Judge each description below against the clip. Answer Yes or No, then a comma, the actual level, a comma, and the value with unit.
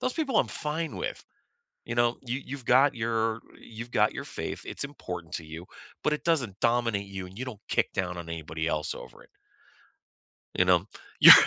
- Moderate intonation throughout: No, wide, 6.3 semitones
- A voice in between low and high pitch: No, low, 115 Hz